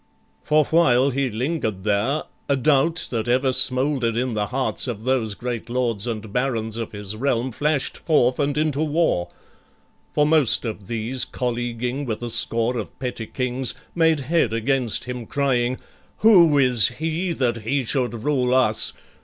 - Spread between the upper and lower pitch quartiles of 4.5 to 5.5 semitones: No, average, 3.5 semitones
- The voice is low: Yes, low, 125 Hz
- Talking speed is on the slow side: No, average, 160 wpm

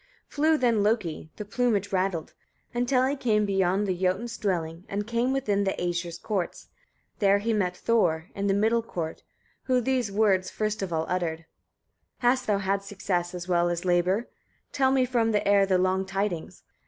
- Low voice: No, high, 200 Hz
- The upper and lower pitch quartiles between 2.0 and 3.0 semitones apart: No, average, 4.0 semitones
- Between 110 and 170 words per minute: No, average, 185 wpm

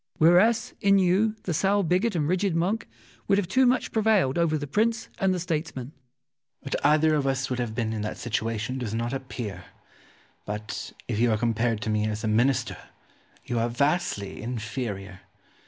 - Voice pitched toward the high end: No, low, 135 Hz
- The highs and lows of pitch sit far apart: Yes, wide, 8.2 semitones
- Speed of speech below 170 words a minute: No, average, 185 wpm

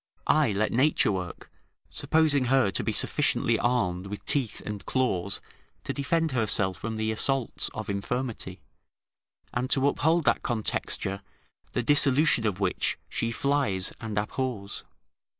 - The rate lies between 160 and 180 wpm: No, slow, 135 wpm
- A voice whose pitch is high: No, low, 115 Hz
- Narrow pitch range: No, average, 5.2 semitones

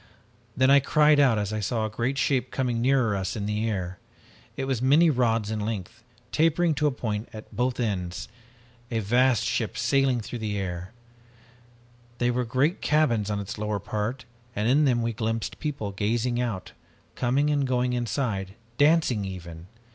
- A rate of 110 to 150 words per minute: No, average, 175 wpm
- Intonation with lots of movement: No, average, 4.1 semitones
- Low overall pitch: Yes, low, 120 Hz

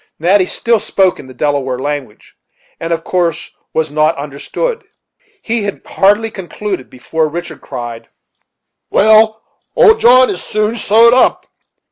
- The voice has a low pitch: No, medium, 185 Hz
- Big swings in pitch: Yes, wide, 6.9 semitones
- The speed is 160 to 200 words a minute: No, slow, 135 wpm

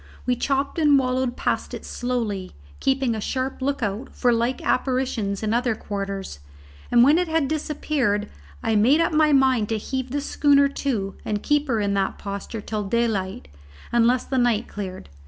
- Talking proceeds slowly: No, average, 175 wpm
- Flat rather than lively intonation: No, average, 4.6 semitones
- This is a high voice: Yes, high, 245 Hz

